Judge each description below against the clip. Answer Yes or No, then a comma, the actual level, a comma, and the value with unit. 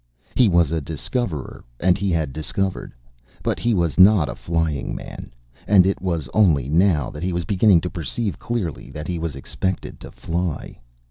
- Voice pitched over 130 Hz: No, very low, 85 Hz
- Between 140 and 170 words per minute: No, average, 180 wpm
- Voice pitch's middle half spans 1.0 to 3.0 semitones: No, average, 3.7 semitones